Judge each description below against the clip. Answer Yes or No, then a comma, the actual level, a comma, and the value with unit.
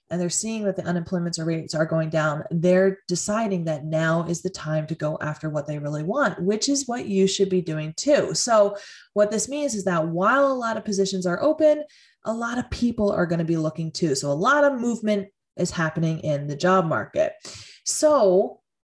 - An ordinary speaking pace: No, fast, 210 wpm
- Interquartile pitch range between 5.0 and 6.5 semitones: Yes, average, 5.3 semitones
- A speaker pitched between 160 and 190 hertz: Yes, medium, 185 Hz